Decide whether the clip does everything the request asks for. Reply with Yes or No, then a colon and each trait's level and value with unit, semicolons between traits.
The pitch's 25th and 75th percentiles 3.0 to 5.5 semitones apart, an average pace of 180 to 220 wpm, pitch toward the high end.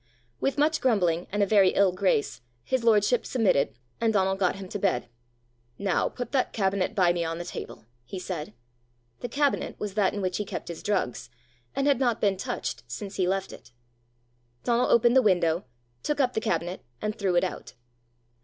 Yes: average, 4.2 semitones; average, 190 wpm; high, 195 Hz